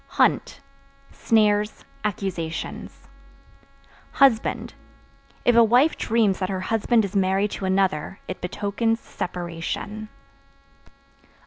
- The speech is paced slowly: Yes, slow, 95 wpm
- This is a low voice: No, high, 205 Hz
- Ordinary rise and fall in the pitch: Yes, average, 3.1 semitones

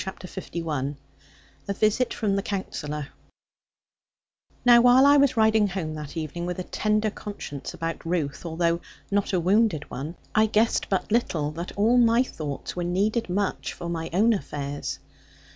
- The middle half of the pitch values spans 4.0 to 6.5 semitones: Yes, average, 5.0 semitones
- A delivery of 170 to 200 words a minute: No, average, 160 wpm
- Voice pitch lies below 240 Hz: Yes, medium, 185 Hz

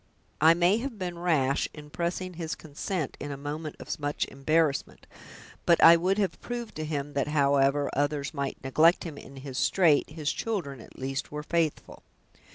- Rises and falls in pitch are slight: No, average, 3.3 semitones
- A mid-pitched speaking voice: Yes, medium, 155 Hz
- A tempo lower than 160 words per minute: No, average, 175 wpm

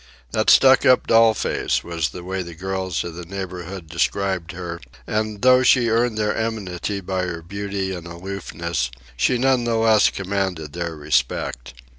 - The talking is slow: No, average, 165 wpm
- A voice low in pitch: Yes, very low, 95 Hz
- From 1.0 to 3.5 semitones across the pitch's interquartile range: No, average, 4.2 semitones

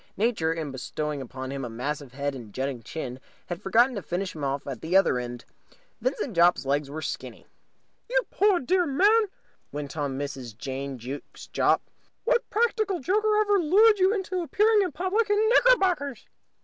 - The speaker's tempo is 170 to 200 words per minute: Yes, average, 175 wpm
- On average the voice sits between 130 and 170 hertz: No, medium, 180 Hz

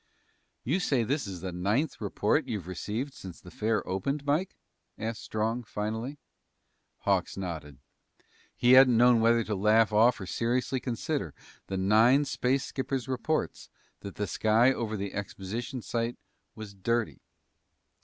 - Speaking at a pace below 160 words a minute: Yes, average, 145 wpm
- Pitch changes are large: No, average, 3.9 semitones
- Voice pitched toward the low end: Yes, low, 115 Hz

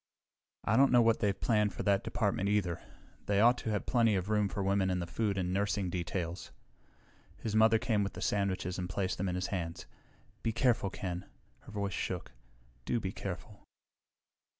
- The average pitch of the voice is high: No, low, 100 Hz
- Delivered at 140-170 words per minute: No, average, 190 wpm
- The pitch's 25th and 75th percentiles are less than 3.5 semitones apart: Yes, average, 2.7 semitones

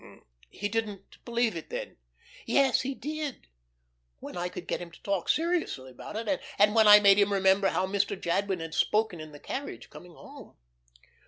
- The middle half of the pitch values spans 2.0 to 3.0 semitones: No, average, 4.3 semitones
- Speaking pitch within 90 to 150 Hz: No, high, 200 Hz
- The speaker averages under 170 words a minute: No, average, 180 wpm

